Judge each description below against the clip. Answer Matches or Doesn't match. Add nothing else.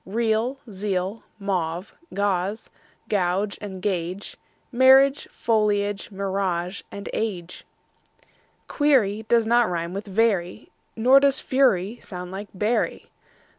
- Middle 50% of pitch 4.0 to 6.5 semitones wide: Doesn't match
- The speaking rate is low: Matches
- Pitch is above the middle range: Matches